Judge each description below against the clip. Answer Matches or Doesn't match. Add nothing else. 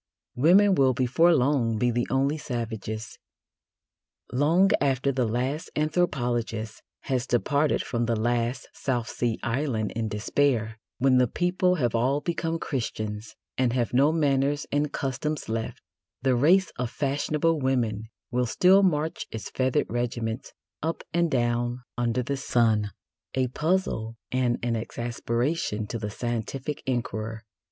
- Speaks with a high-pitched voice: Doesn't match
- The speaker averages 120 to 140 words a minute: Matches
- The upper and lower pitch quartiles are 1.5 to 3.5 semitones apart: Doesn't match